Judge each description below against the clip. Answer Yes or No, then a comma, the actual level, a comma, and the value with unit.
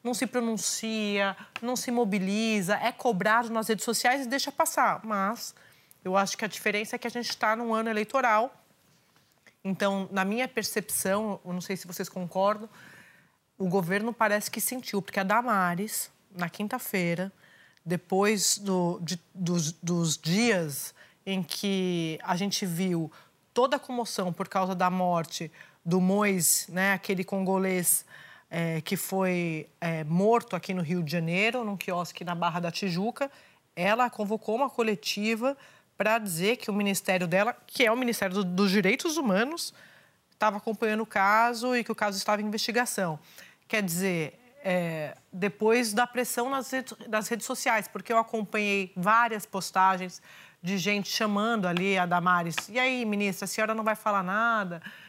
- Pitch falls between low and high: No, high, 205 Hz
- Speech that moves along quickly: No, average, 160 wpm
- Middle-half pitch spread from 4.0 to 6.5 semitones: No, average, 3.5 semitones